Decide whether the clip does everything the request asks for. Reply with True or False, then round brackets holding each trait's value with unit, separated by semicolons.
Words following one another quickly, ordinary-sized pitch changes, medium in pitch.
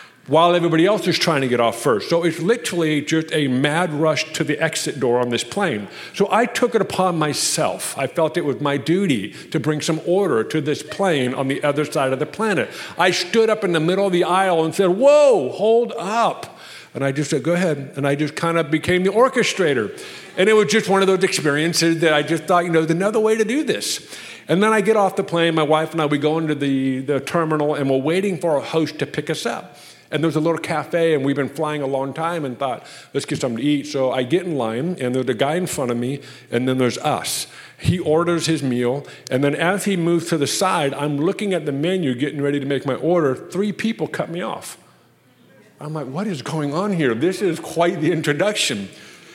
True (245 wpm; 4.2 semitones; 160 Hz)